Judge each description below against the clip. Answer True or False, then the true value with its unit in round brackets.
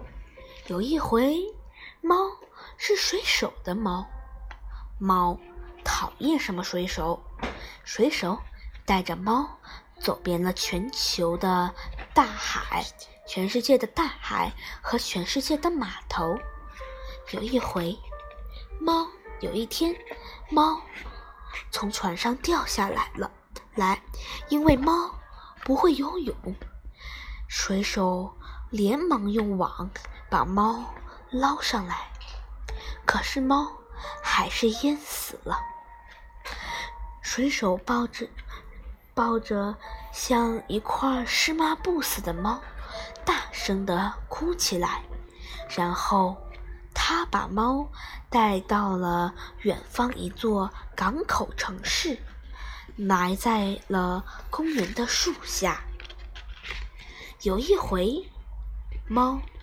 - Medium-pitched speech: False (230 Hz)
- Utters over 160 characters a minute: False (135 characters per minute)